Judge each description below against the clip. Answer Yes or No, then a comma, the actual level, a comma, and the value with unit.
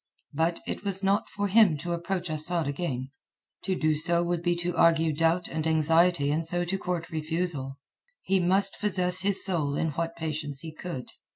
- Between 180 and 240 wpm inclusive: Yes, average, 185 wpm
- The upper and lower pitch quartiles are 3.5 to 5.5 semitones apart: No, narrow, 2.5 semitones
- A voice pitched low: No, medium, 170 Hz